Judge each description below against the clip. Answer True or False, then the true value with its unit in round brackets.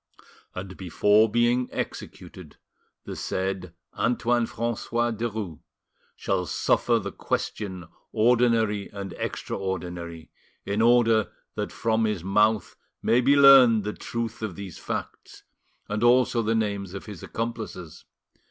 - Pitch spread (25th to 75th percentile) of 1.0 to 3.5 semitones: True (3.2 semitones)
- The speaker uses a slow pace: True (120 wpm)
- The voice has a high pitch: False (110 Hz)